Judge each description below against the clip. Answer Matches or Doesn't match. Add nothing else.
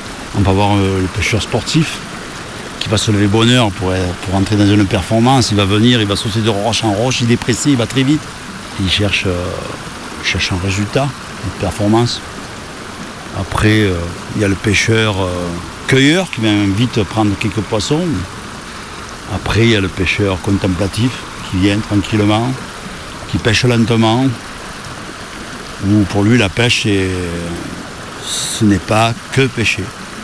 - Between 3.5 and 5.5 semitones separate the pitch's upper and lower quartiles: Doesn't match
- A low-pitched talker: Matches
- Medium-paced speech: Matches